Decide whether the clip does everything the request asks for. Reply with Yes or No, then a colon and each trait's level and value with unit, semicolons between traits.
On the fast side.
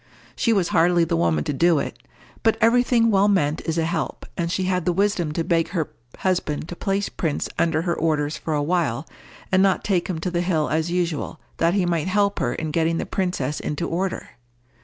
Yes: fast, 220 wpm